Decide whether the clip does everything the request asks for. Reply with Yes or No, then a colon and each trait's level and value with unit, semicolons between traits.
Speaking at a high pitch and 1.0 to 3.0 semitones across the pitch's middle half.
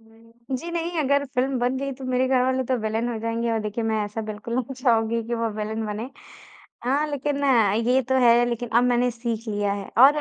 Yes: high, 240 Hz; narrow, 2.6 semitones